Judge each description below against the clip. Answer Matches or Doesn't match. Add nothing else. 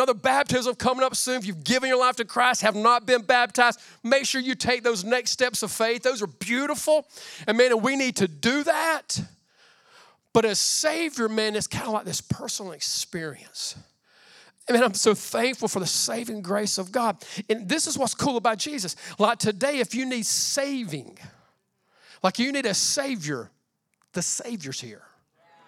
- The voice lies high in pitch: Matches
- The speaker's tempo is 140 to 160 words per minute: Doesn't match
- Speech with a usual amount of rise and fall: Matches